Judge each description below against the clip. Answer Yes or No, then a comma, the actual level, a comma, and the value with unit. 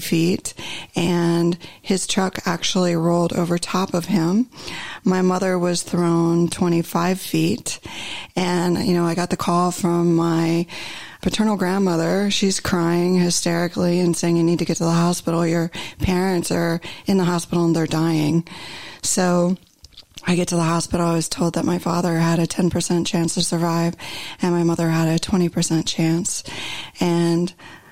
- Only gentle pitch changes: Yes, narrow, 1.1 semitones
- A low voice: No, medium, 175 Hz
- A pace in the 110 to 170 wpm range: Yes, average, 160 wpm